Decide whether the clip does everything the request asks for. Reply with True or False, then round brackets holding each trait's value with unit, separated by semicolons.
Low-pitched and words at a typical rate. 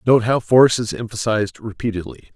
True (110 Hz; 155 wpm)